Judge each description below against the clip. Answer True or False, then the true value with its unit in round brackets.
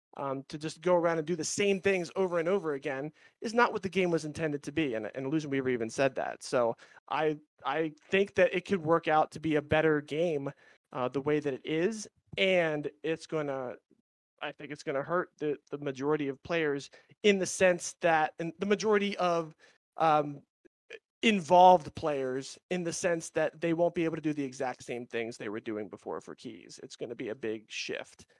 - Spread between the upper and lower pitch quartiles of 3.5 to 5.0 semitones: True (4.1 semitones)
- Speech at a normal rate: False (210 wpm)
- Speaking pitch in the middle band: True (160 Hz)